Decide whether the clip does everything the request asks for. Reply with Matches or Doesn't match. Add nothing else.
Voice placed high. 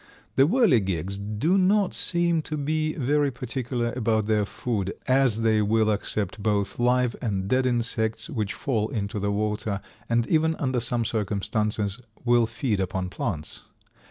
Doesn't match